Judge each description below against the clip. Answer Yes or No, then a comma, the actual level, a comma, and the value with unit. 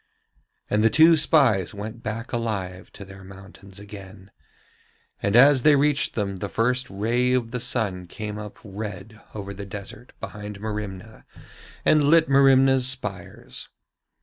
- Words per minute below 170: Yes, average, 145 wpm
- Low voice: Yes, low, 110 Hz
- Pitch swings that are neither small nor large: Yes, average, 4.2 semitones